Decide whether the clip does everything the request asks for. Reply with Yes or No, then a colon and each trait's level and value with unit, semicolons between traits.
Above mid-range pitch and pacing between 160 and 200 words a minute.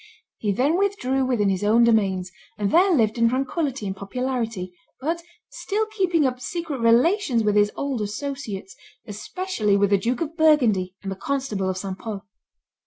Yes: high, 235 Hz; average, 170 wpm